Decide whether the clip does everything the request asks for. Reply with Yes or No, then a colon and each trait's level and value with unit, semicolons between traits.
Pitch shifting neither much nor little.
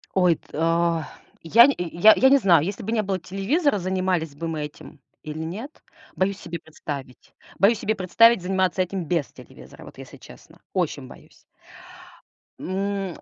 Yes: average, 3.4 semitones